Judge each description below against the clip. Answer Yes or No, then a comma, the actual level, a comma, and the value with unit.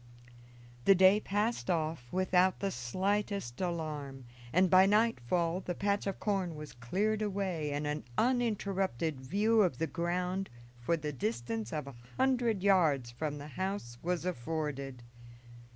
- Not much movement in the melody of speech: No, average, 5.3 semitones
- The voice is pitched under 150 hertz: No, medium, 175 Hz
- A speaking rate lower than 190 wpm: Yes, average, 140 wpm